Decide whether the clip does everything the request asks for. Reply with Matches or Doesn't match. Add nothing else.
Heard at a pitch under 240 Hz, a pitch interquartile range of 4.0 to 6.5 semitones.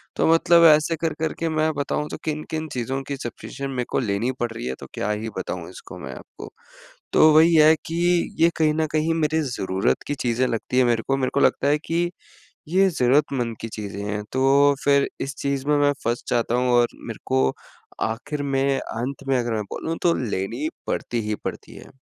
Matches